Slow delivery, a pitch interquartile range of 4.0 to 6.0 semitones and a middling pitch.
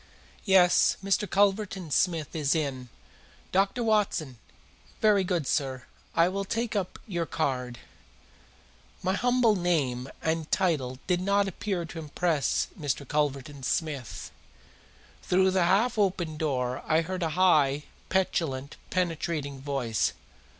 Yes: slow, 120 wpm; average, 5.2 semitones; medium, 165 Hz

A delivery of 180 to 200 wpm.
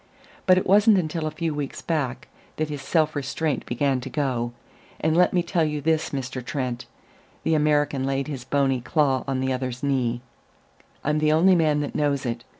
Yes: average, 190 wpm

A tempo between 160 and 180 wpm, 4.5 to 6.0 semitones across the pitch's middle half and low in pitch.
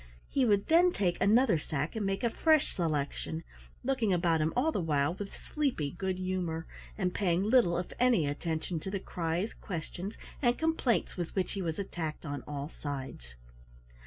No: average, 175 wpm; wide, 5.4 semitones; medium, 180 Hz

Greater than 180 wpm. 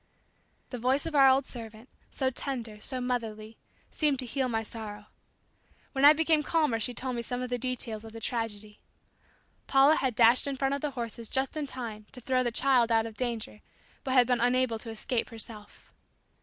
Yes: average, 195 wpm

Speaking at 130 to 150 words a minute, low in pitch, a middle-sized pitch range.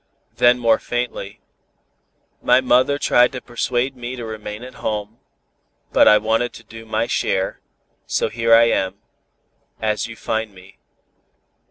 No: average, 145 wpm; low, 115 Hz; narrow, 2.2 semitones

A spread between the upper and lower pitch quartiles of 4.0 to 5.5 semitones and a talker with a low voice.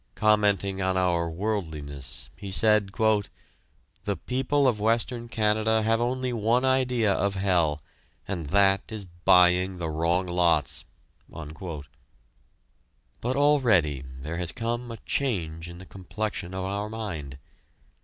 Yes: average, 4.5 semitones; low, 100 Hz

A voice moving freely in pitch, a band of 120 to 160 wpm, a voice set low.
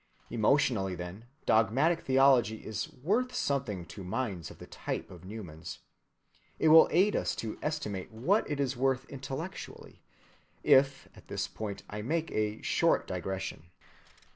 Yes: wide, 6.3 semitones; average, 140 wpm; low, 120 Hz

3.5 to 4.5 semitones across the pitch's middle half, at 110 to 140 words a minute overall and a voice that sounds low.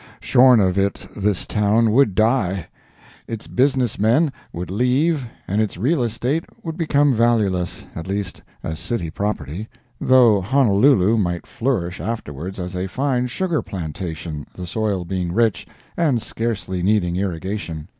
No: wide, 5.5 semitones; slow, 135 wpm; low, 105 Hz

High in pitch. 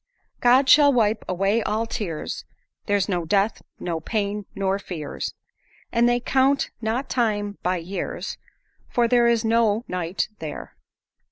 Yes: high, 210 Hz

